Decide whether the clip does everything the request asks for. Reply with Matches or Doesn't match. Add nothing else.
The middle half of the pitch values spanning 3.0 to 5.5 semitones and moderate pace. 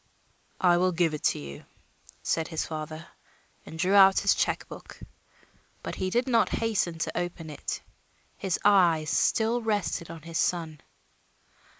Matches